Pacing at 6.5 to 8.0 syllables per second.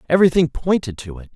Yes: 7.0 syllables/s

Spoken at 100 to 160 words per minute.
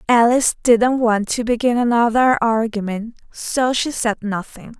Yes: average, 140 wpm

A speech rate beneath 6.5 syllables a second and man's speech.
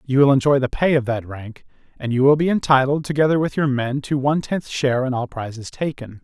Yes: 5.9 syllables/s; male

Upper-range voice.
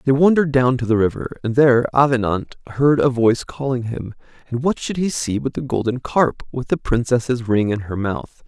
No: low, 125 Hz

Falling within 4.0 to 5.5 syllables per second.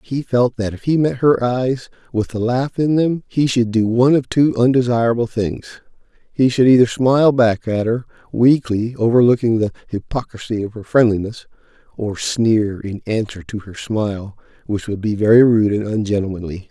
Yes: 5.0 syllables/s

